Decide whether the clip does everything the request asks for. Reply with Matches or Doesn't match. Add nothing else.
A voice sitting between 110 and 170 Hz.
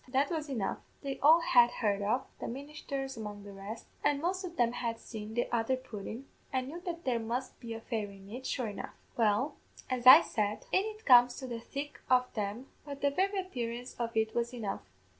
Doesn't match